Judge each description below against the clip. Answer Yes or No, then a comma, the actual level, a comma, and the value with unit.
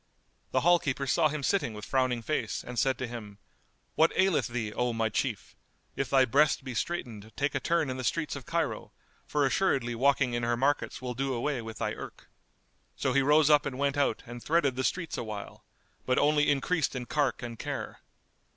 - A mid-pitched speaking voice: No, low, 130 Hz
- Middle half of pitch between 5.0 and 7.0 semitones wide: No, average, 3.6 semitones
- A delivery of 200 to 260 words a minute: Yes, fast, 205 wpm